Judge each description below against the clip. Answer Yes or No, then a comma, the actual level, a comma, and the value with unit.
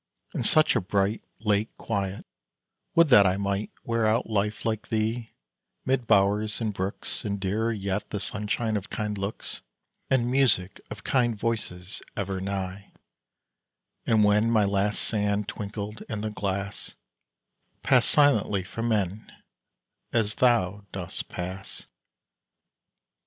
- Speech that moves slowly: Yes, slow, 130 wpm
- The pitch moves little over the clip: Yes, narrow, 2.3 semitones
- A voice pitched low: Yes, low, 105 Hz